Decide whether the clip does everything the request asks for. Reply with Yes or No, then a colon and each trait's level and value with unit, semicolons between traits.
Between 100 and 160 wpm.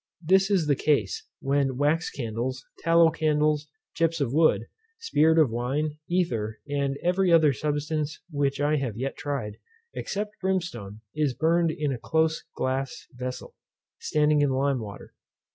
Yes: average, 145 wpm